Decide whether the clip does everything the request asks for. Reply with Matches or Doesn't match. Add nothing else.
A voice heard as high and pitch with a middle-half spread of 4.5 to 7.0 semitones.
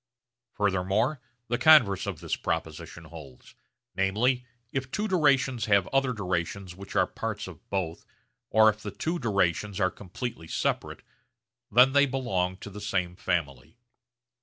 Doesn't match